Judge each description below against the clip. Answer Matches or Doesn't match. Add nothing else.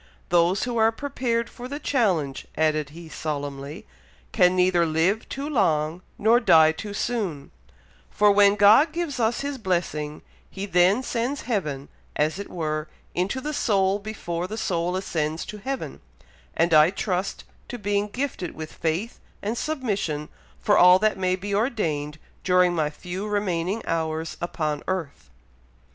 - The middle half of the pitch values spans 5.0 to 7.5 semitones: Matches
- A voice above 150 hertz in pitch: Matches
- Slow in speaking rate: Doesn't match